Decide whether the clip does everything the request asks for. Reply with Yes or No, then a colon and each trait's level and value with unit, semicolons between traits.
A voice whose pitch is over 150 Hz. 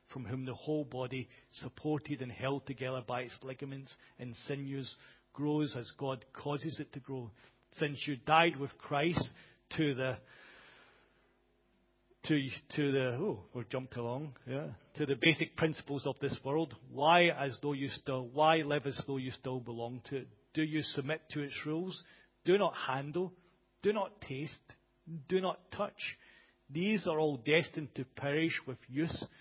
No: medium, 140 Hz